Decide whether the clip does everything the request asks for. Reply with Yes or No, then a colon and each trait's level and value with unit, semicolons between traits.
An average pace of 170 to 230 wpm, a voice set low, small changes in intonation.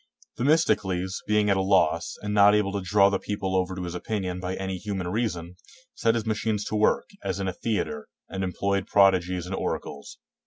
Yes: average, 200 wpm; very low, 95 Hz; narrow, 2.3 semitones